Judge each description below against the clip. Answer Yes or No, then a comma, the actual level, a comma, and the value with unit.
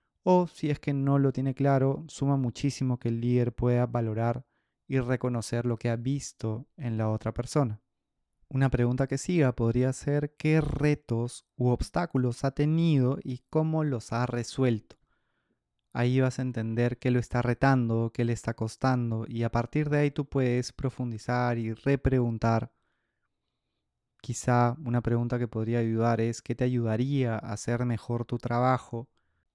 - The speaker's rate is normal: Yes, average, 160 wpm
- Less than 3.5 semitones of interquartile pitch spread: Yes, narrow, 2.6 semitones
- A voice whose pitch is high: No, low, 125 Hz